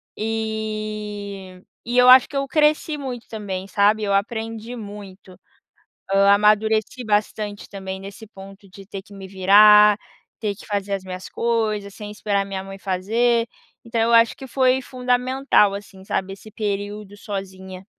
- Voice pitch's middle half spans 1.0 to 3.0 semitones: Yes, narrow, 2.4 semitones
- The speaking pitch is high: Yes, high, 210 Hz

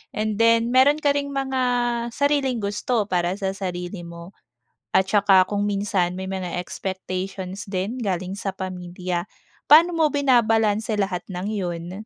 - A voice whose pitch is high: Yes, high, 200 Hz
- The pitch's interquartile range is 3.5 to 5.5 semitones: Yes, average, 3.9 semitones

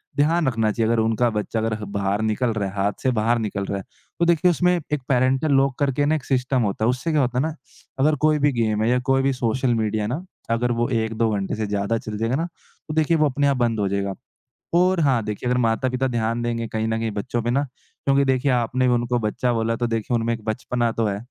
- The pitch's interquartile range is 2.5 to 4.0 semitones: Yes, average, 3.3 semitones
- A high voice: No, low, 120 Hz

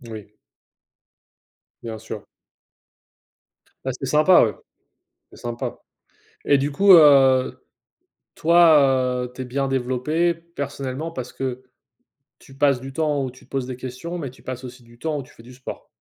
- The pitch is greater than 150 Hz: No, low, 135 Hz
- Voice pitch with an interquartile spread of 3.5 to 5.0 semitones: No, average, 3.0 semitones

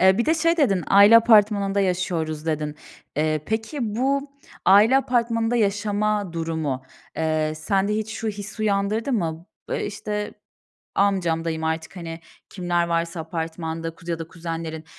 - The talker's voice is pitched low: No, high, 190 Hz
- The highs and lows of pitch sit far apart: No, average, 4.8 semitones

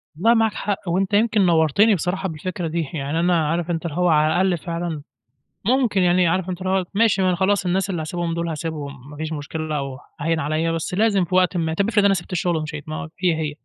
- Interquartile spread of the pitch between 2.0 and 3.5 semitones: Yes, average, 3.1 semitones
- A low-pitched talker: No, medium, 175 Hz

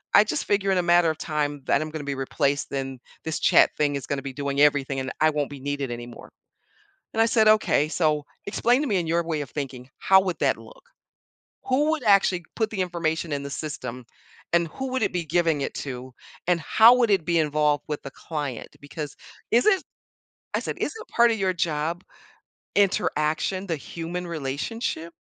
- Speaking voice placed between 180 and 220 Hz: No, medium, 160 Hz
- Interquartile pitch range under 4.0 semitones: No, average, 5.0 semitones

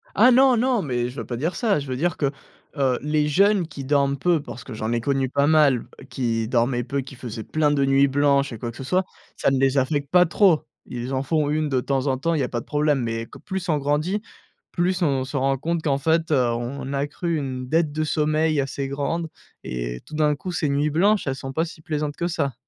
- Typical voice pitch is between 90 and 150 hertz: Yes, medium, 140 Hz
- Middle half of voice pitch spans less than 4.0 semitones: Yes, average, 3.3 semitones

